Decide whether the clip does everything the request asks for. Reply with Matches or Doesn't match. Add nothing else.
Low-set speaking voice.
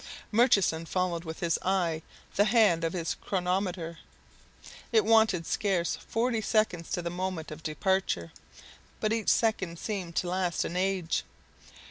Doesn't match